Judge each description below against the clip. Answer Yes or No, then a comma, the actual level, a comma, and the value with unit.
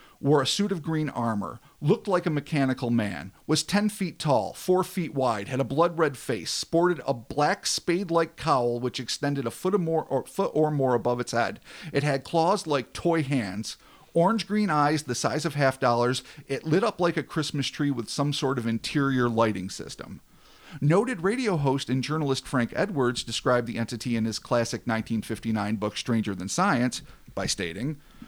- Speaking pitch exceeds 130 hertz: Yes, medium, 140 Hz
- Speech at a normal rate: Yes, average, 190 wpm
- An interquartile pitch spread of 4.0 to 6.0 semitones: Yes, average, 5.3 semitones